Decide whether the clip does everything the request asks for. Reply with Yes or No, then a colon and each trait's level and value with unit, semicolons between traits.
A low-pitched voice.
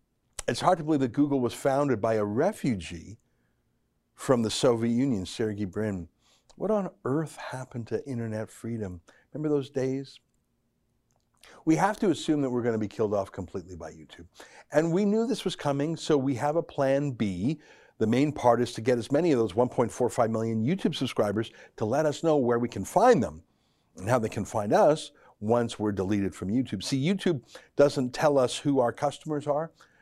Yes: low, 125 Hz